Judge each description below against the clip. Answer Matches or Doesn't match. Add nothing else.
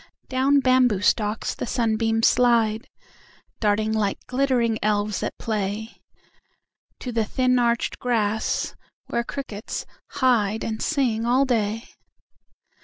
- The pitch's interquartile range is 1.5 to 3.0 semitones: Matches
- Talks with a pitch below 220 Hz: Doesn't match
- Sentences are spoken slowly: Matches